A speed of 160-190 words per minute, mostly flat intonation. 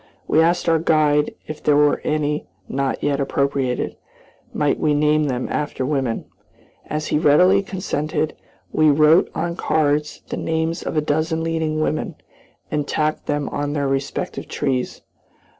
No: average, 150 wpm; narrow, 1.5 semitones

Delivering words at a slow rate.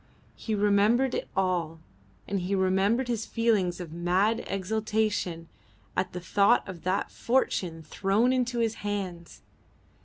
Yes: slow, 130 wpm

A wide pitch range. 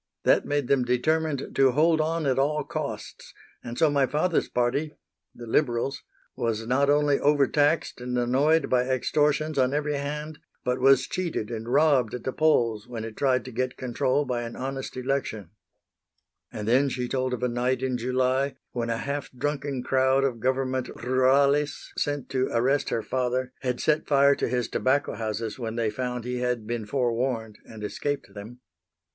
No: average, 2.7 semitones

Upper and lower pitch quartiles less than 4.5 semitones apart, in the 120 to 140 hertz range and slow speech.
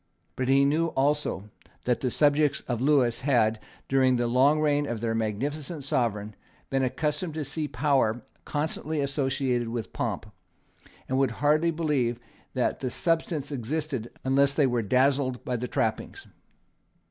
No: average, 3.5 semitones; low, 135 Hz; average, 145 wpm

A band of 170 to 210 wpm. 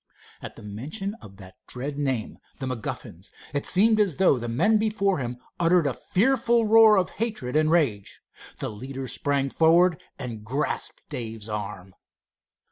No: average, 155 wpm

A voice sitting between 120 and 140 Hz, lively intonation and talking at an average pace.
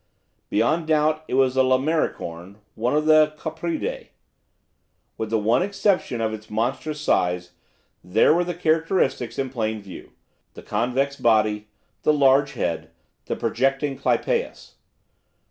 No: low, 135 Hz; wide, 6.0 semitones; slow, 130 wpm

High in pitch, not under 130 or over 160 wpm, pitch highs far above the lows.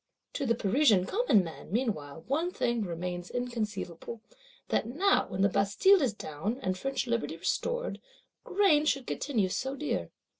Yes: high, 230 Hz; average, 150 wpm; wide, 7.0 semitones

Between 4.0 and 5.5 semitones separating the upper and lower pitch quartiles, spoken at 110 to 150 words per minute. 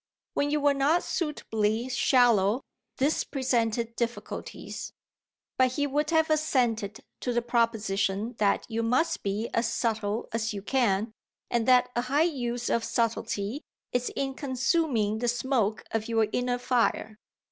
No: average, 3.2 semitones; average, 145 wpm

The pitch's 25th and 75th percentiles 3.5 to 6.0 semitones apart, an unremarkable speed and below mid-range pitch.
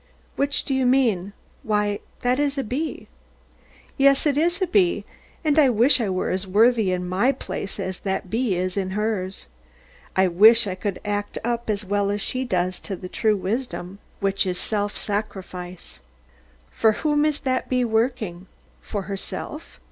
No: average, 5.2 semitones; average, 170 wpm; high, 210 Hz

